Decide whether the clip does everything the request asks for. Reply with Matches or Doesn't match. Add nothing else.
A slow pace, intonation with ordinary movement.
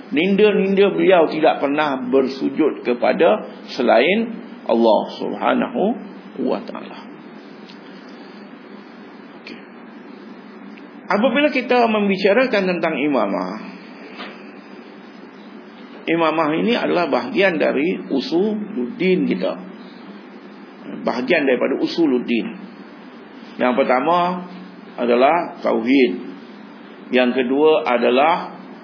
Doesn't match